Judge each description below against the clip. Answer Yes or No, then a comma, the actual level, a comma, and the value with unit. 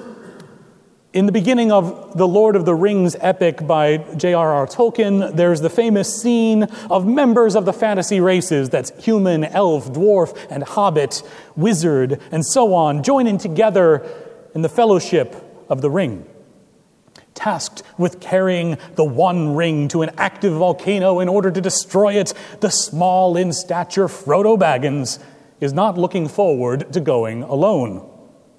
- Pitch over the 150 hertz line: Yes, medium, 185 Hz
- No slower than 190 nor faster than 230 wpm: No, average, 145 wpm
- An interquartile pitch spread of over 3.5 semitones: Yes, average, 4.2 semitones